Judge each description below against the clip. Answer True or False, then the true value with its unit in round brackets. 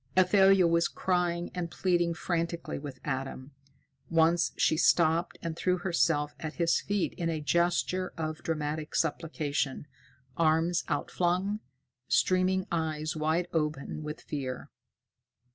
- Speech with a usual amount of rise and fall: False (2.3 semitones)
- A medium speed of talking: False (120 wpm)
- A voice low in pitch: False (165 Hz)